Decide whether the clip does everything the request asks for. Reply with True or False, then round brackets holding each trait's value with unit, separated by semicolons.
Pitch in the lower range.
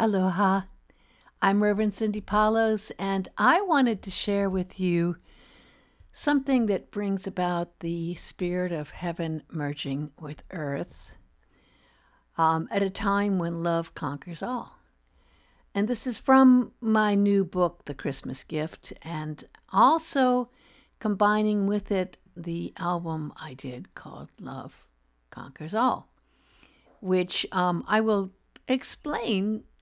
False (190 Hz)